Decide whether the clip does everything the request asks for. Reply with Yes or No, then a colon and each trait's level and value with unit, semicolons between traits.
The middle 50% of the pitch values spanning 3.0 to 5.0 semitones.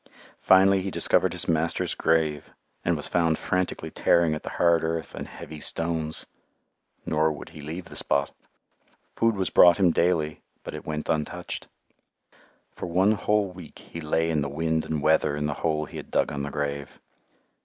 No: narrow, 2.4 semitones